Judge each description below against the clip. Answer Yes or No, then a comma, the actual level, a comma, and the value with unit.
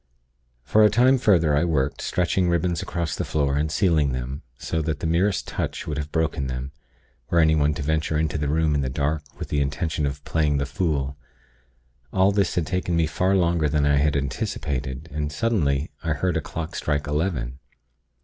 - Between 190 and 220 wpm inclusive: Yes, average, 195 wpm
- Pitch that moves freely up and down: No, average, 3.0 semitones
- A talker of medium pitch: No, very low, 75 Hz